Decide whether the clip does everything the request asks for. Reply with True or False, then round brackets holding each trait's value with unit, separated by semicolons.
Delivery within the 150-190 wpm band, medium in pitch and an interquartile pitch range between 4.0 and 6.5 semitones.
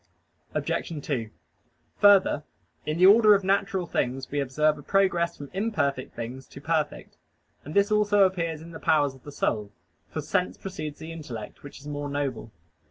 True (170 wpm; 155 Hz; 5.3 semitones)